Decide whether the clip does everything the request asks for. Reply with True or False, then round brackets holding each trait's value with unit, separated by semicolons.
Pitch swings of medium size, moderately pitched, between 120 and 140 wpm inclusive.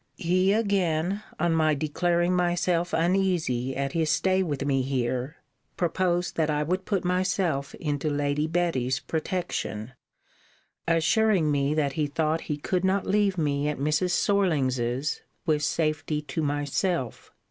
True (3.8 semitones; 160 Hz; 135 wpm)